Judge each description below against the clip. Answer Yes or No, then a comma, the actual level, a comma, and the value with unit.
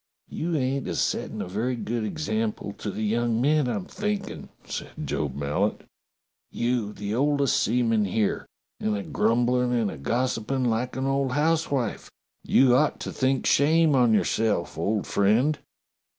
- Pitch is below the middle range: Yes, low, 120 Hz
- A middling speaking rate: Yes, average, 150 wpm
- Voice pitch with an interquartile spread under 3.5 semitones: No, average, 4.1 semitones